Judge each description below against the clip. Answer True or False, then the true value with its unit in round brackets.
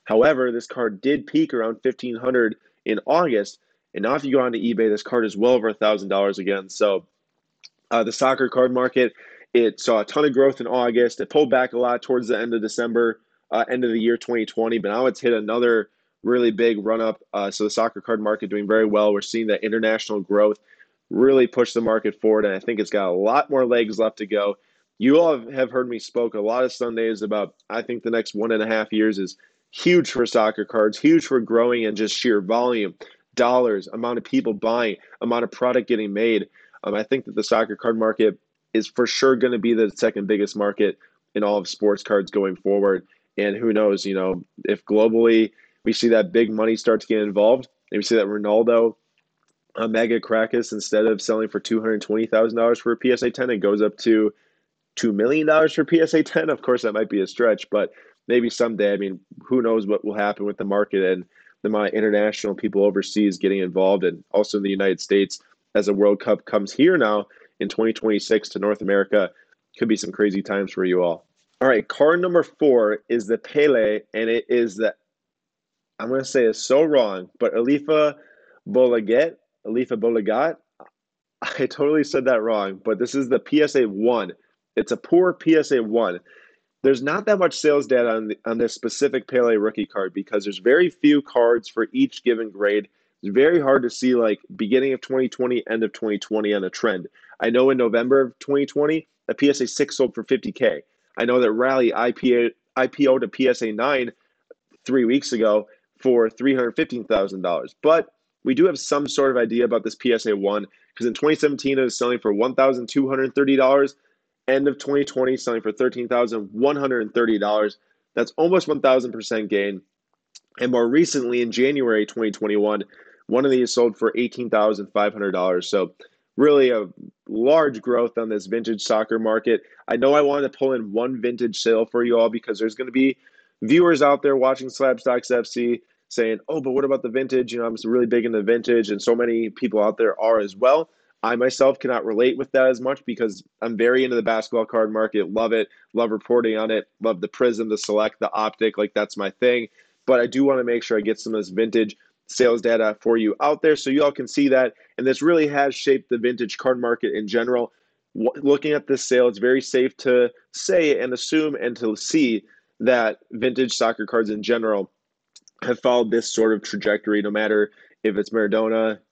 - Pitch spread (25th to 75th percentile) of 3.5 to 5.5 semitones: False (3.0 semitones)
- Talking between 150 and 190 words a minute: False (205 wpm)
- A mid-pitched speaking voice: False (115 Hz)